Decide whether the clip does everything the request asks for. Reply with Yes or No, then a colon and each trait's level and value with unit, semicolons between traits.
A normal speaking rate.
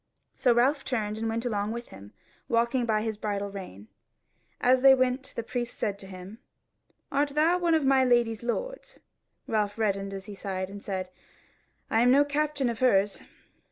Yes: average, 185 wpm